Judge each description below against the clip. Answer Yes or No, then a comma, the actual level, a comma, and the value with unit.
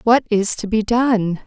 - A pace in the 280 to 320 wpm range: No, fast, 205 wpm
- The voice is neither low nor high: No, high, 220 Hz